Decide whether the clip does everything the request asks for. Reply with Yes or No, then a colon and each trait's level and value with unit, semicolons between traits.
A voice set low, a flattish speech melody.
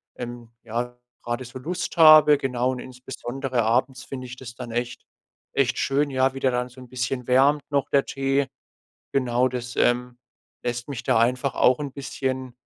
Yes: low, 130 Hz; narrow, 1.8 semitones